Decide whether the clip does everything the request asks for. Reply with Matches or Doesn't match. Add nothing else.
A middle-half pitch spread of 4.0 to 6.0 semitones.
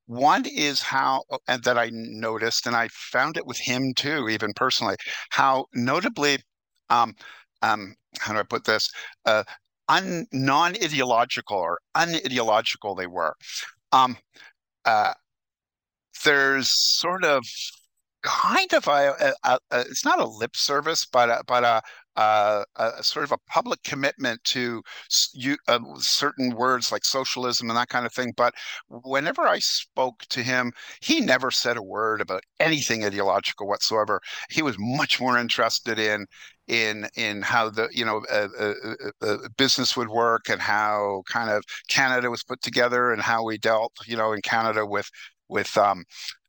Doesn't match